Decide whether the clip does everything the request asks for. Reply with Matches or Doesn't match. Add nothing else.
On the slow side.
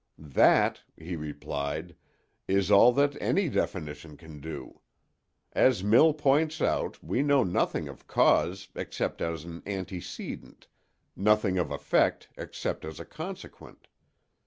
Matches